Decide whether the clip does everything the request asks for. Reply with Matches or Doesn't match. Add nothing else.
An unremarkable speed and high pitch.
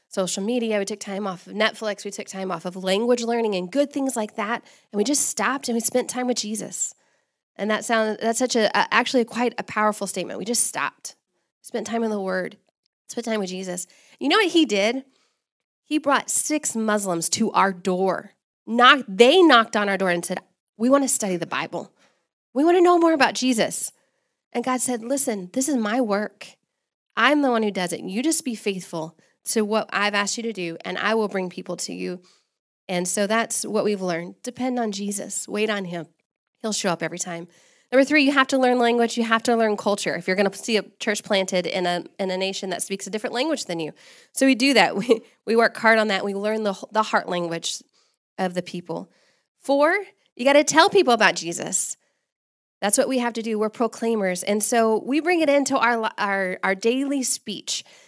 Doesn't match